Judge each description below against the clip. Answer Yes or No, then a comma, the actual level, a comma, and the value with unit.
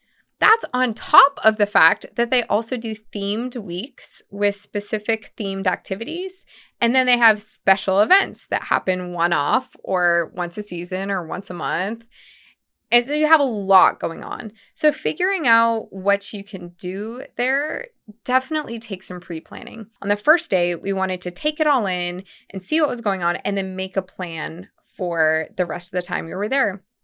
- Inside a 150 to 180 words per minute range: No, average, 195 wpm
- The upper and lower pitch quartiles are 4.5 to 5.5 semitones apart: Yes, average, 4.8 semitones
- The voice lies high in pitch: Yes, high, 205 Hz